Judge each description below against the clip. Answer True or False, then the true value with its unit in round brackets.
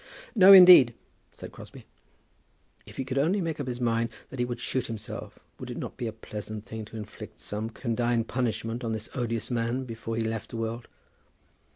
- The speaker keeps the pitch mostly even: True (2.3 semitones)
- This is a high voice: False (115 Hz)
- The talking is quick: False (195 wpm)